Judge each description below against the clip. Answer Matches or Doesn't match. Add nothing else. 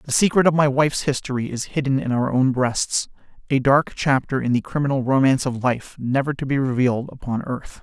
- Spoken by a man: Matches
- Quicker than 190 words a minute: Matches